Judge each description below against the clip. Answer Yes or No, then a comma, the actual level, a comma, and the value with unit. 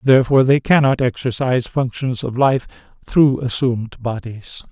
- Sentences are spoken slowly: Yes, slow, 125 wpm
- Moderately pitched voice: No, low, 125 Hz